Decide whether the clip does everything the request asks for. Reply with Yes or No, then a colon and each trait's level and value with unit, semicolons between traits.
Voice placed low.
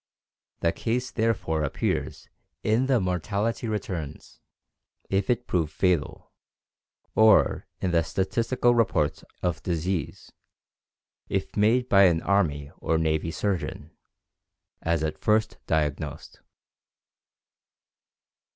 Yes: very low, 95 Hz